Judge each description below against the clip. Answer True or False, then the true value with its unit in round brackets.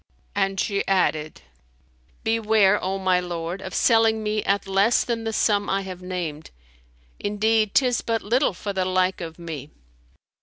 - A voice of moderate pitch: False (195 Hz)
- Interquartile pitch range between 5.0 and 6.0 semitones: False (3.1 semitones)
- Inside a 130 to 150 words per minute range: False (160 wpm)